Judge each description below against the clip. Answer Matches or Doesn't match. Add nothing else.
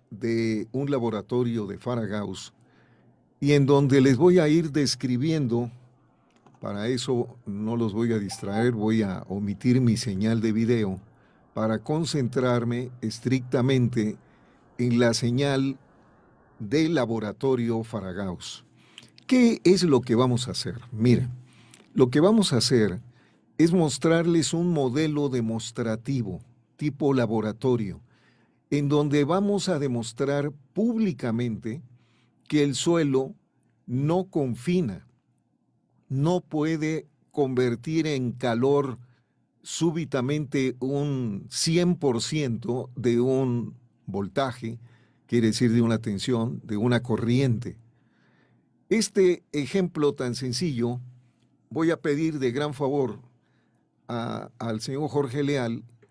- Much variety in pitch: Doesn't match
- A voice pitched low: Matches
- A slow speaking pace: Matches